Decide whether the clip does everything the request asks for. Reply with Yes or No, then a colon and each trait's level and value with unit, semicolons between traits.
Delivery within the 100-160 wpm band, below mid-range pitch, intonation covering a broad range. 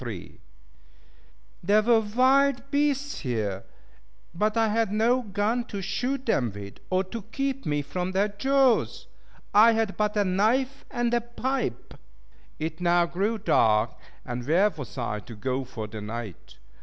No: average, 150 wpm; high, 205 Hz; wide, 8.6 semitones